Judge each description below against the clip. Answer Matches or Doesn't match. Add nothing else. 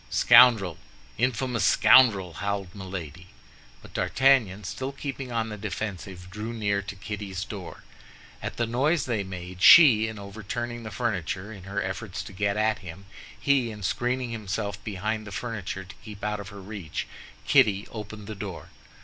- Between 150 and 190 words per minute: Matches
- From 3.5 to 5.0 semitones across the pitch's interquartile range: Doesn't match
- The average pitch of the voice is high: Doesn't match